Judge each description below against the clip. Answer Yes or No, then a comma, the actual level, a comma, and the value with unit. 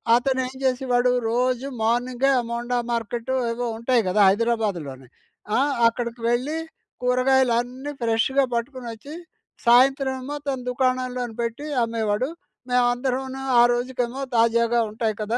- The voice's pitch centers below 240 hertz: No, high, 245 Hz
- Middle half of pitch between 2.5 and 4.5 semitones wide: No, narrow, 1.9 semitones